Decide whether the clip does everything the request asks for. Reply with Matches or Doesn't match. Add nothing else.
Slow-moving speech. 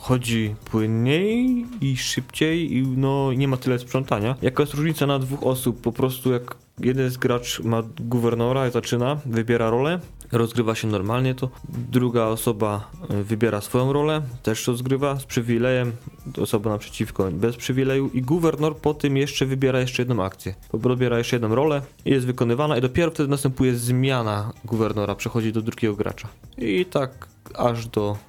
Doesn't match